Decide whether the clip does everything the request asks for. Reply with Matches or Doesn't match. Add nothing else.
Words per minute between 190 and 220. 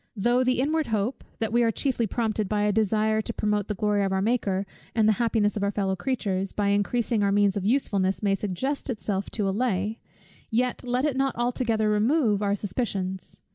Matches